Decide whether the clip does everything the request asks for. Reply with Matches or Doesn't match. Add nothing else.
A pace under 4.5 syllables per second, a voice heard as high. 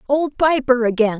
Doesn't match